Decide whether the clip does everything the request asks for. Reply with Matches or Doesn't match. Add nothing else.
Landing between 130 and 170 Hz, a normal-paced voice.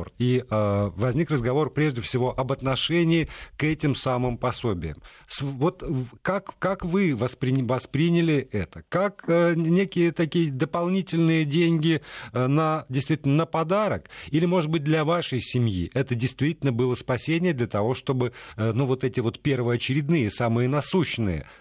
Matches